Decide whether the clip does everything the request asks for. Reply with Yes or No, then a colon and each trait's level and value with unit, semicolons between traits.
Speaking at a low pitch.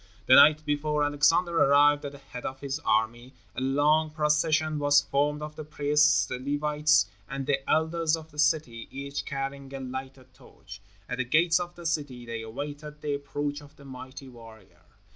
No: medium, 145 Hz